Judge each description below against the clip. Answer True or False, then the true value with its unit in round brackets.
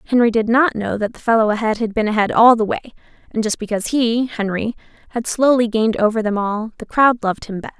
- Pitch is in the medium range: False (225 Hz)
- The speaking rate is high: True (215 wpm)